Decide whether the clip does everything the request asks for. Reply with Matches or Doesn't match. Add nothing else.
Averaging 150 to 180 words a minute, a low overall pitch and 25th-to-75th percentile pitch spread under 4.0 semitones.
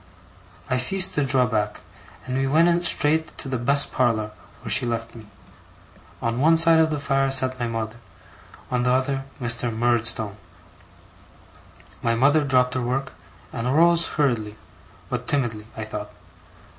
Matches